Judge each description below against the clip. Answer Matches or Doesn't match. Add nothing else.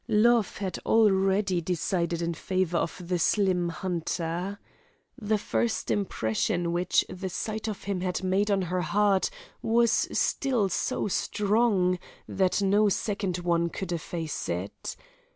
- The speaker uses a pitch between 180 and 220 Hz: Matches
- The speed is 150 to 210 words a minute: Doesn't match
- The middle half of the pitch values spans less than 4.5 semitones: Matches